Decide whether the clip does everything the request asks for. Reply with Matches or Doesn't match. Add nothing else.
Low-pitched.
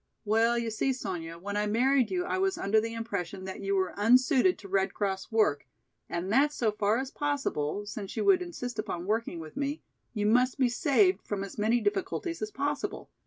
Doesn't match